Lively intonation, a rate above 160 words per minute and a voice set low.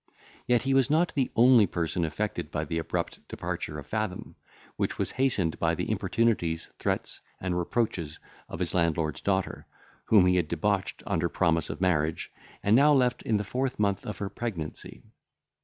Yes: wide, 6.1 semitones; average, 175 wpm; very low, 95 Hz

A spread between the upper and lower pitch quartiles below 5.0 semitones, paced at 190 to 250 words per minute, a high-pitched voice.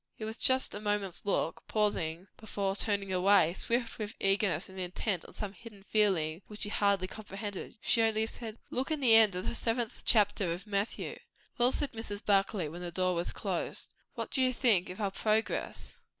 Yes: average, 2.9 semitones; average, 195 wpm; high, 205 Hz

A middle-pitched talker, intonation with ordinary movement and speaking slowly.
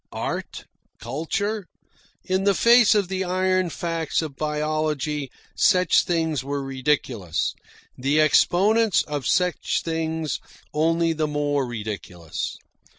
Yes: medium, 155 Hz; average, 4.2 semitones; slow, 110 wpm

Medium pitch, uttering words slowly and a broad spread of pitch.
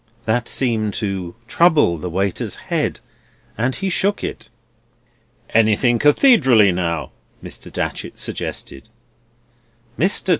No: low, 110 Hz; slow, 105 wpm; wide, 7.7 semitones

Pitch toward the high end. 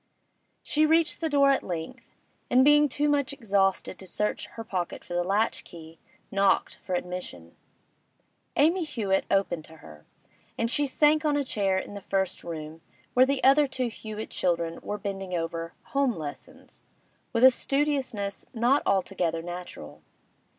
Yes: high, 205 Hz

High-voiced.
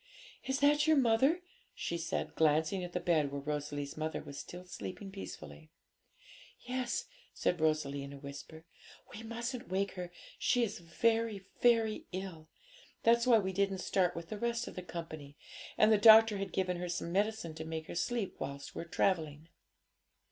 No: medium, 180 Hz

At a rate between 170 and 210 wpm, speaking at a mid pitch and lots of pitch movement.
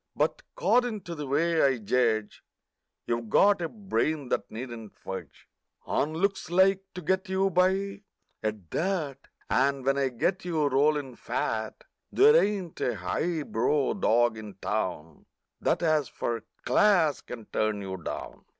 No: average, 145 wpm; medium, 145 Hz; wide, 8.0 semitones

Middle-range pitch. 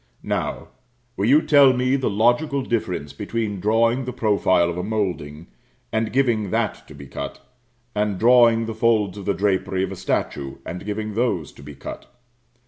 No: low, 105 Hz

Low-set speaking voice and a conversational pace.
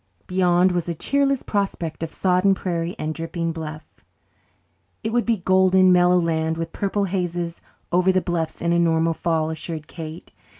No: medium, 175 Hz; average, 170 wpm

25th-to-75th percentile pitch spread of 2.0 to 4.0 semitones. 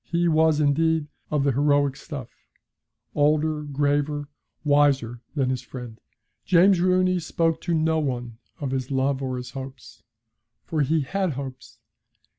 Yes: average, 3.2 semitones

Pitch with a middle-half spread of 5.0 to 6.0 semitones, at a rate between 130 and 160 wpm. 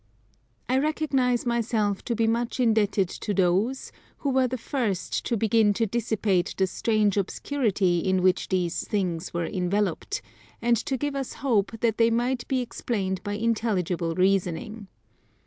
No: average, 4.1 semitones; average, 150 wpm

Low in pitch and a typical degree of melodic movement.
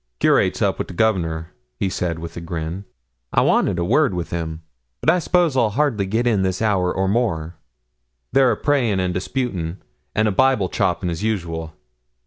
No: very low, 95 Hz; wide, 5.7 semitones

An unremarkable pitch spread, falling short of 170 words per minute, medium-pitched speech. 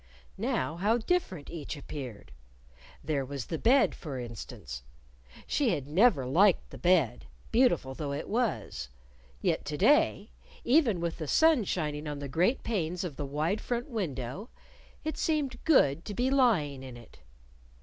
No: wide, 8.9 semitones; average, 155 wpm; medium, 165 Hz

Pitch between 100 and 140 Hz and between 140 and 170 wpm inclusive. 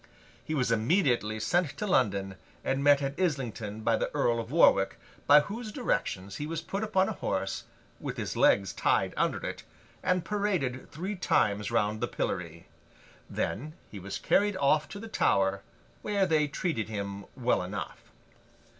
Yes: low, 135 Hz; average, 165 wpm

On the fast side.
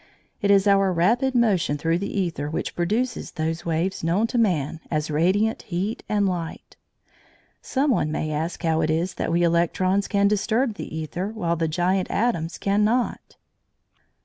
No: average, 165 wpm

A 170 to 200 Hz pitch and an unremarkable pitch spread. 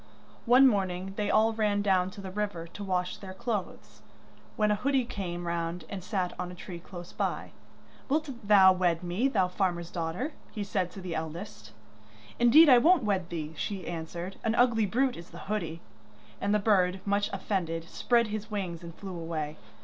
Yes: high, 190 Hz; average, 3.5 semitones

